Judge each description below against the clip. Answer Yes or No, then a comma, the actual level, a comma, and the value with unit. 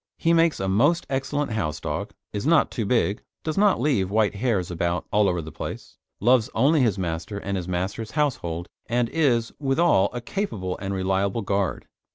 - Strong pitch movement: Yes, wide, 6.0 semitones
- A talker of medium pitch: No, low, 110 Hz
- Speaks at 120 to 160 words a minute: No, average, 185 wpm